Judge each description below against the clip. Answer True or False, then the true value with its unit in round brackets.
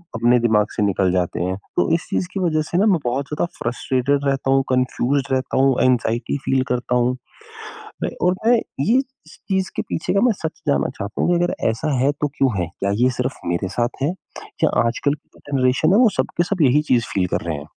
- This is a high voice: False (130 Hz)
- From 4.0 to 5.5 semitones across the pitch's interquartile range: True (4.4 semitones)